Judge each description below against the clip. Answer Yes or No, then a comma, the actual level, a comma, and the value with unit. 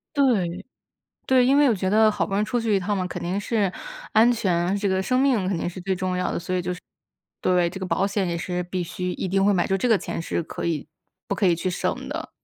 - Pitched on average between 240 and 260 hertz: No, high, 190 Hz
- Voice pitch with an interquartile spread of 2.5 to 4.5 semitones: Yes, average, 2.9 semitones